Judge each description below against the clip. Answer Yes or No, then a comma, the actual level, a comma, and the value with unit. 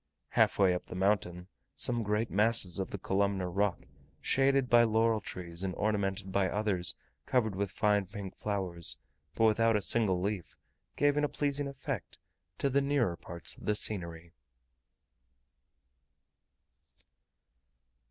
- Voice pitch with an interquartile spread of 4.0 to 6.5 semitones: No, average, 3.6 semitones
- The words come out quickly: No, average, 140 wpm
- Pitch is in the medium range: No, low, 100 Hz